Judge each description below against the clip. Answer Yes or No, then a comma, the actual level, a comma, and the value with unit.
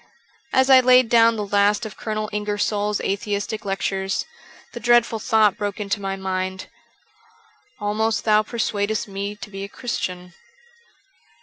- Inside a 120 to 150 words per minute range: Yes, average, 140 wpm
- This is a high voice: Yes, high, 210 Hz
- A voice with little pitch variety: Yes, narrow, 2.3 semitones